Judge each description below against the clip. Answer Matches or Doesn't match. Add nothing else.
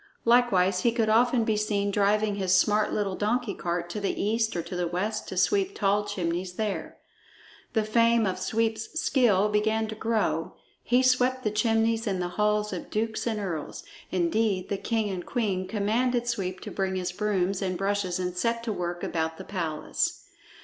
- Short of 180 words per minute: Doesn't match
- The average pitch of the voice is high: Matches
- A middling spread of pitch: Matches